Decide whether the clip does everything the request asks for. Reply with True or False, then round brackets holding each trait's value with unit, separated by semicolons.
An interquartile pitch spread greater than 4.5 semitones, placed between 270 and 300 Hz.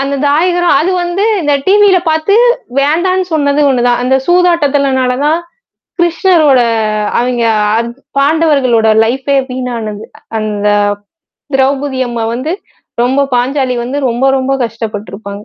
True (4.9 semitones; 275 Hz)